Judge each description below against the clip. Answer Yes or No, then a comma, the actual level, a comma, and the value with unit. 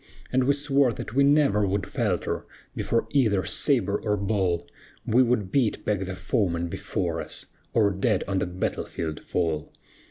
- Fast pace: No, average, 165 wpm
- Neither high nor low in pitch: No, low, 105 Hz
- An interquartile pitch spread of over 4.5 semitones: Yes, average, 5.1 semitones